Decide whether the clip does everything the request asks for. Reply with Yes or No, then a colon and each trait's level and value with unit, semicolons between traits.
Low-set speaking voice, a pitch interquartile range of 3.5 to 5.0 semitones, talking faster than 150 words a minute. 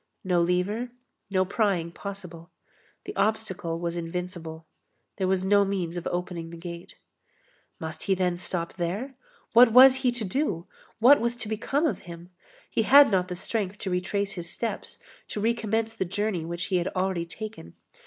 No: high, 190 Hz; average, 4.0 semitones; average, 170 wpm